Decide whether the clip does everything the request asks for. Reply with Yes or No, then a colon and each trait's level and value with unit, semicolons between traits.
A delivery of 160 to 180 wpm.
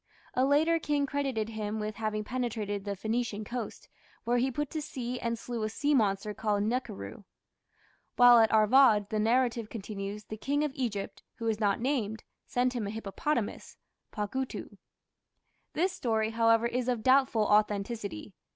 Yes: average, 165 wpm